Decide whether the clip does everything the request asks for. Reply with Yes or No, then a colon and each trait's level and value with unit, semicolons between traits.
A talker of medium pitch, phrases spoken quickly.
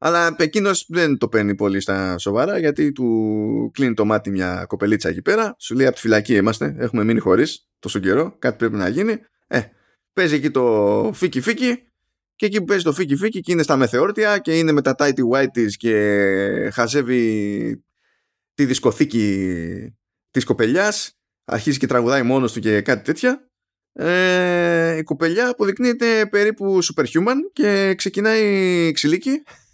No: medium, 145 Hz; average, 155 wpm